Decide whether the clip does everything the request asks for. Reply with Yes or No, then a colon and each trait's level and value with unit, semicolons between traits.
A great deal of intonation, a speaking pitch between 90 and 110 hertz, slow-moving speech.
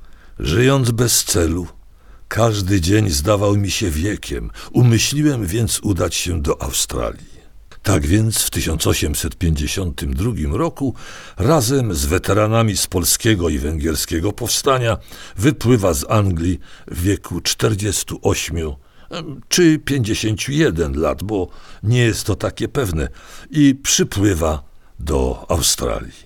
Yes: wide, 5.7 semitones; low, 100 Hz; slow, 105 wpm